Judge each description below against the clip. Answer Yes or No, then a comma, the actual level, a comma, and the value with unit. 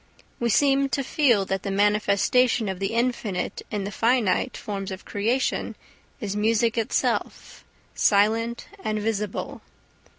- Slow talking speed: Yes, slow, 130 wpm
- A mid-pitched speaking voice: No, high, 215 Hz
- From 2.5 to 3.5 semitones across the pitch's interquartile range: Yes, average, 2.9 semitones